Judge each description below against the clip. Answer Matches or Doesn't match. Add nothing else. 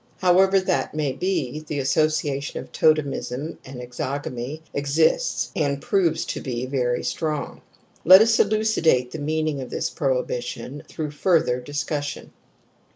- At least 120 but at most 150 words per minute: Matches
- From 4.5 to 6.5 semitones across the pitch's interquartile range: Doesn't match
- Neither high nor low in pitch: Matches